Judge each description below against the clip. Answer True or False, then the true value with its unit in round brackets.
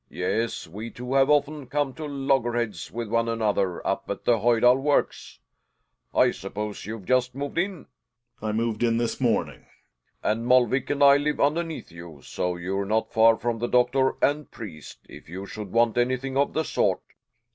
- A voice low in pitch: True (120 Hz)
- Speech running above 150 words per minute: True (180 wpm)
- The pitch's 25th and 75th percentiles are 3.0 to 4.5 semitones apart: True (4.0 semitones)